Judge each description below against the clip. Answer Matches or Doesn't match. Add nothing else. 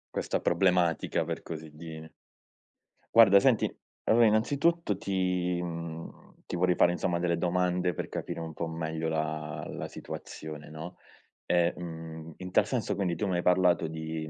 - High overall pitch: Doesn't match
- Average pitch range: Doesn't match